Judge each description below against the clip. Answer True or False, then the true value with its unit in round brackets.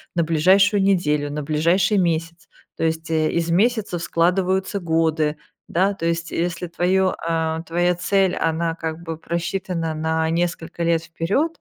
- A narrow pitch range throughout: True (2.1 semitones)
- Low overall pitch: False (170 Hz)